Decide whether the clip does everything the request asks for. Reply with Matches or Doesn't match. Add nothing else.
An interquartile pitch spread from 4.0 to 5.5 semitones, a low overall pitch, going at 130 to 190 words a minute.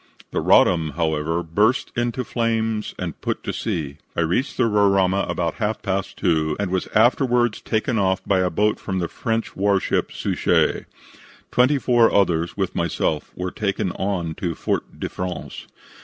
Matches